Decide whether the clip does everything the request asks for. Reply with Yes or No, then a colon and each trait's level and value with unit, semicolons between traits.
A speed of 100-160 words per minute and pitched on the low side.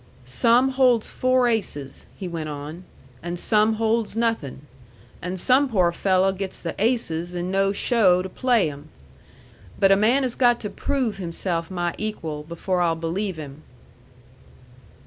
No: average, 150 wpm; high, 190 Hz